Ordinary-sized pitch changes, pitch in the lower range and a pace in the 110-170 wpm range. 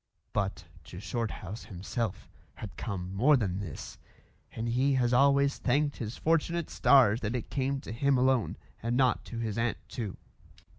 Yes: average, 4.6 semitones; low, 120 Hz; average, 160 wpm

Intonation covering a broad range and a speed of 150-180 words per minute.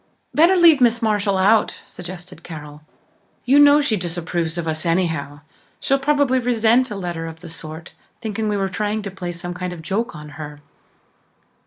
Yes: wide, 5.7 semitones; average, 175 wpm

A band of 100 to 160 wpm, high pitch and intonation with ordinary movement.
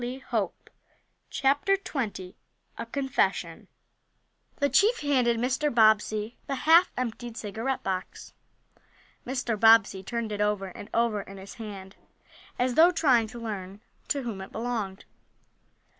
Yes: slow, 135 wpm; high, 230 Hz; average, 4.2 semitones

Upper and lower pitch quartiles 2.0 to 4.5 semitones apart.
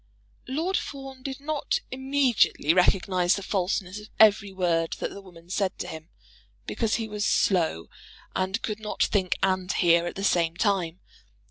Yes: average, 3.8 semitones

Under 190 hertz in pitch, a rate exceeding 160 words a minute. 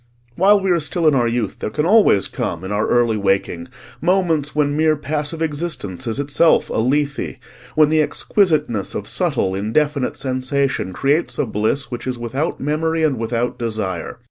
Yes: medium, 140 Hz; average, 170 wpm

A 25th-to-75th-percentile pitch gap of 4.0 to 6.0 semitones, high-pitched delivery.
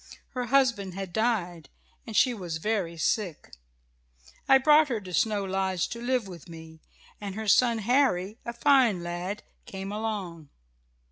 Yes: average, 4.9 semitones; high, 205 Hz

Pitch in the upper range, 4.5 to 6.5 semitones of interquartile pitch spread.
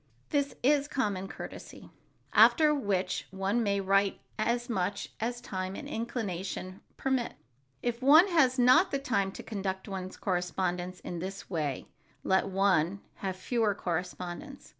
Yes: high, 200 Hz; average, 4.8 semitones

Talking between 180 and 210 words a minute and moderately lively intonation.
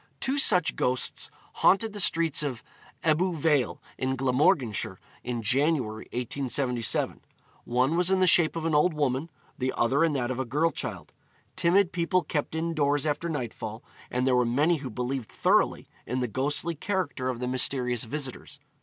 No: average, 165 wpm; average, 4.7 semitones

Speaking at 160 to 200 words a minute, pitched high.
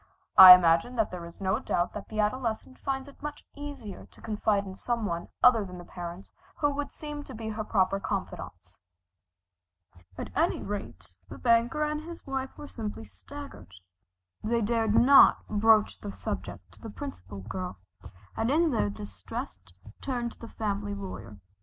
Yes: average, 170 wpm; high, 215 Hz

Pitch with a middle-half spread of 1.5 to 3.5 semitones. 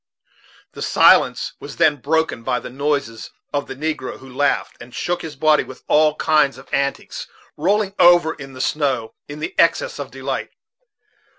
Yes: average, 3.0 semitones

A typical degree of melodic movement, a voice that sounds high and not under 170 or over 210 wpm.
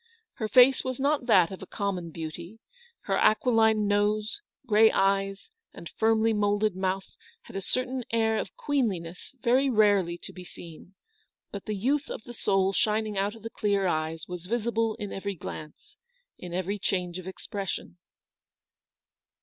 No: average, 3.2 semitones; high, 205 Hz; average, 160 wpm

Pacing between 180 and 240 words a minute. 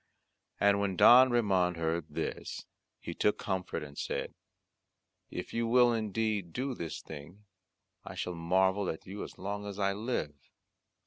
No: average, 150 wpm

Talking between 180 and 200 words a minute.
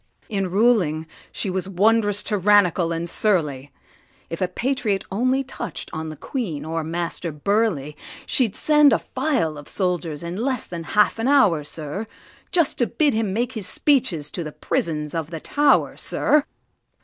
No: average, 160 wpm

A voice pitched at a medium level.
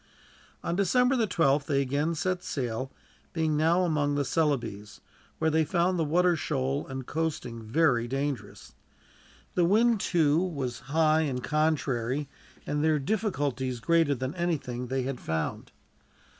Yes: medium, 150 Hz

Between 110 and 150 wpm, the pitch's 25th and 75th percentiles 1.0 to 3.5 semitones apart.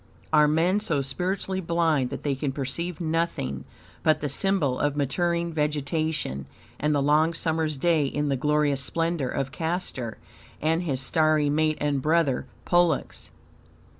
Yes: average, 145 wpm; average, 3.1 semitones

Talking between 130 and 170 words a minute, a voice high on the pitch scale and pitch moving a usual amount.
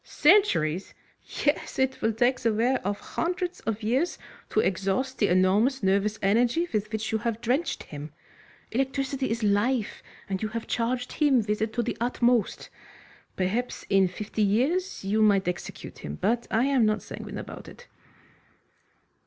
Yes: average, 160 wpm; high, 225 Hz; average, 4.1 semitones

